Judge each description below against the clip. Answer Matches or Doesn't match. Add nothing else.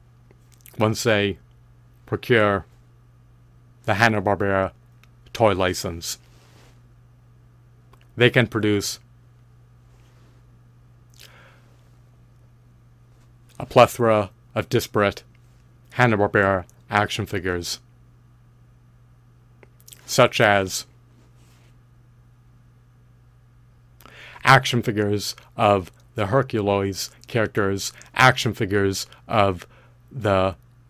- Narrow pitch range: Matches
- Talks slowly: Matches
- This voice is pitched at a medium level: Doesn't match